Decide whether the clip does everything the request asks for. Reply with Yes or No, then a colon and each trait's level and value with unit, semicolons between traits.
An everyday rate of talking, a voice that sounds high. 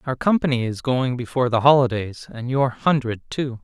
No: average, 180 wpm; low, 125 Hz